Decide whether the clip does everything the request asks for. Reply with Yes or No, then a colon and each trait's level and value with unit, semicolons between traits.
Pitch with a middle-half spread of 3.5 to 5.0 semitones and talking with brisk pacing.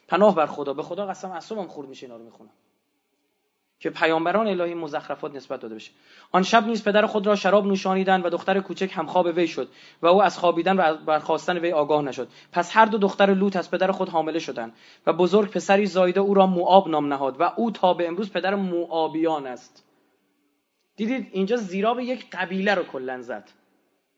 Yes: average, 4.1 semitones; fast, 190 wpm